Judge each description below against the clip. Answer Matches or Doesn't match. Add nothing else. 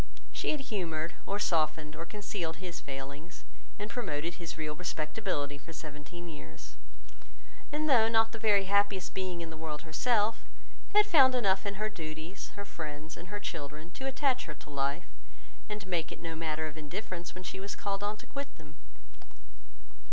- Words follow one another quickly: Doesn't match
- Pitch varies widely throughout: Doesn't match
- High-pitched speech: Doesn't match